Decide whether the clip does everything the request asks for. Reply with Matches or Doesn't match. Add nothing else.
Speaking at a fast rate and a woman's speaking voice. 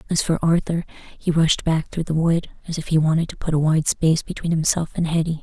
Matches